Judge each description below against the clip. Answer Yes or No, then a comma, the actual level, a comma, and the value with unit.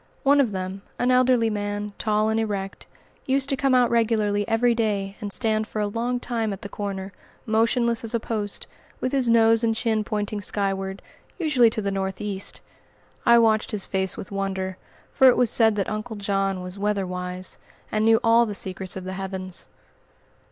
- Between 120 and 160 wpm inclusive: No, average, 185 wpm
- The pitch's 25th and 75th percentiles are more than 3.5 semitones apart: No, average, 2.8 semitones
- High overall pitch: Yes, high, 215 Hz